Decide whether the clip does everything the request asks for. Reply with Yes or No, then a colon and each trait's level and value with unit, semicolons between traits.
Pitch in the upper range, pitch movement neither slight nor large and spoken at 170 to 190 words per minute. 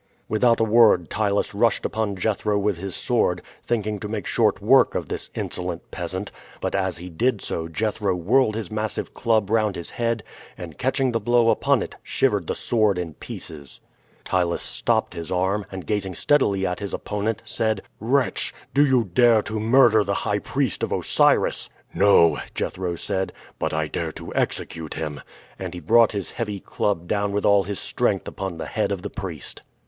No: low, 100 Hz; average, 3.4 semitones; average, 185 wpm